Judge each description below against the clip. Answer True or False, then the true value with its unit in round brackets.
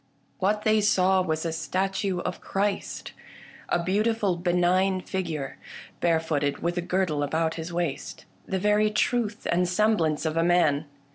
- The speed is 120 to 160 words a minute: True (150 wpm)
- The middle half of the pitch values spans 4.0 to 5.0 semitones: False (3.1 semitones)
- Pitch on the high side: False (180 Hz)